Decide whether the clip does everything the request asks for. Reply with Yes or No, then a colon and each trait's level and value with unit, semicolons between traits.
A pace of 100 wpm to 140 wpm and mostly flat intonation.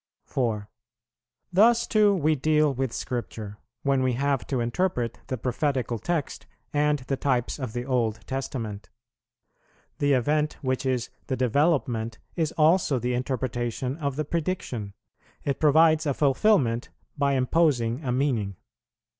No: slow, 135 wpm; average, 3.8 semitones